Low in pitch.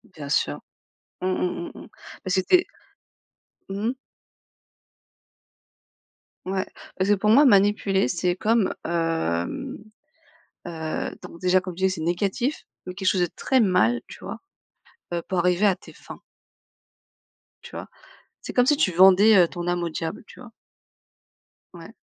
No: medium, 185 Hz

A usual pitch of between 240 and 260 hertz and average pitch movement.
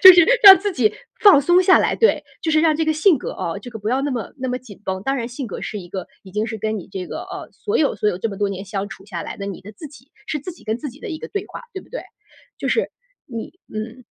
No: high, 245 Hz; wide, 7.4 semitones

